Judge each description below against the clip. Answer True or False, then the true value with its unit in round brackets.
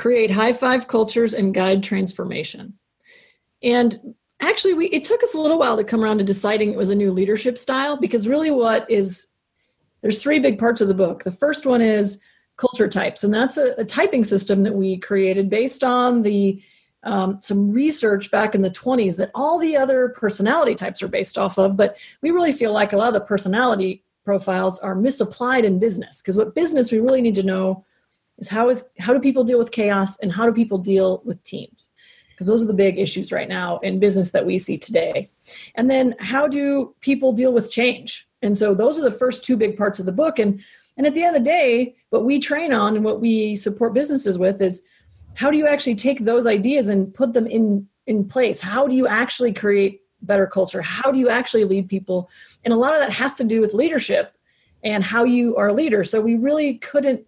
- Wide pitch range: False (4.2 semitones)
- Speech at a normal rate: False (220 wpm)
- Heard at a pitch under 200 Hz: False (225 Hz)